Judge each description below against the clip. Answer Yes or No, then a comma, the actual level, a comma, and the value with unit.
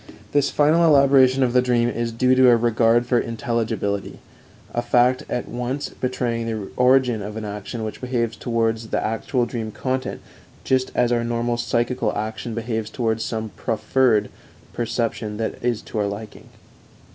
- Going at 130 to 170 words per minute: Yes, average, 160 wpm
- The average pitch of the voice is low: Yes, low, 120 Hz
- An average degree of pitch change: No, narrow, 2.1 semitones